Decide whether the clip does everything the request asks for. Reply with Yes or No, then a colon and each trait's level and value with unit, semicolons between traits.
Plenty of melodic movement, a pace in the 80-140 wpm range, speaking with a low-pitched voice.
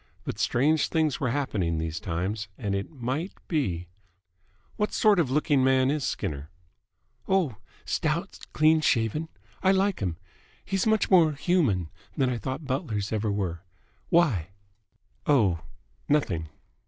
Yes: wide, 8.0 semitones; slow, 135 wpm; low, 130 Hz